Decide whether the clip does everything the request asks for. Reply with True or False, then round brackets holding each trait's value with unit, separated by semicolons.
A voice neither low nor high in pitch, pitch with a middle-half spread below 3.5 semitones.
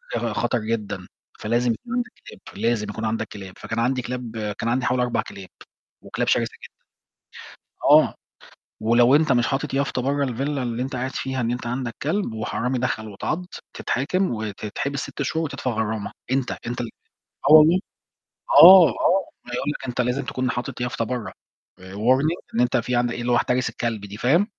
False (125 Hz; 3.0 semitones)